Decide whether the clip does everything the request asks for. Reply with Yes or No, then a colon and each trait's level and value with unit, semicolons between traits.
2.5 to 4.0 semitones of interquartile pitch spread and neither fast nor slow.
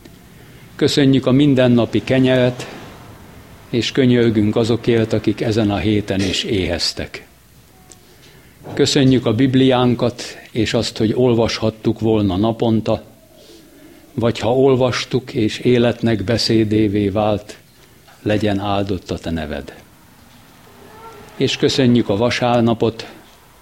No: average, 2.8 semitones; slow, 95 wpm